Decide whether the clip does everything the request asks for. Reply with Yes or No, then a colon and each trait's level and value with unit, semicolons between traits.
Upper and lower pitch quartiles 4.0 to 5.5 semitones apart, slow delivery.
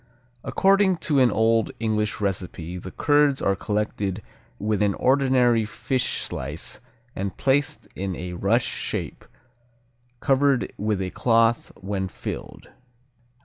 Yes: average, 5.1 semitones; slow, 120 wpm